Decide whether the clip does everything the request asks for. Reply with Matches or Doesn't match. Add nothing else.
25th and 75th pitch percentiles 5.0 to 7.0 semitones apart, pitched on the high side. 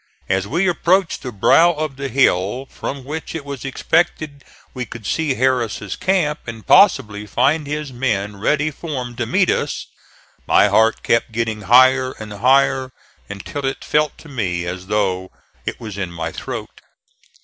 Doesn't match